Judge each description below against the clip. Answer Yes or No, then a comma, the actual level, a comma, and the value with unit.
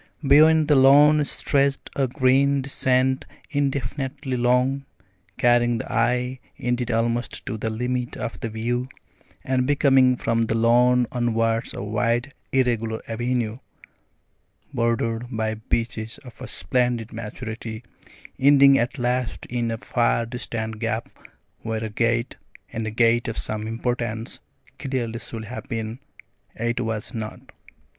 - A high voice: No, low, 120 Hz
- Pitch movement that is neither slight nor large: No, narrow, 2.3 semitones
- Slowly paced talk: Yes, slow, 130 wpm